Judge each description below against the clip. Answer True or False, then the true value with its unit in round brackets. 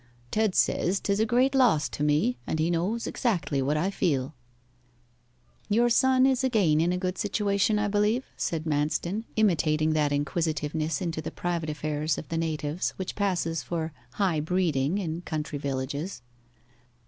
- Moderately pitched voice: True (165 Hz)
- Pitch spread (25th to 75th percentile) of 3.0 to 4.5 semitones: False (5.0 semitones)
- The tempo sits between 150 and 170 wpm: True (160 wpm)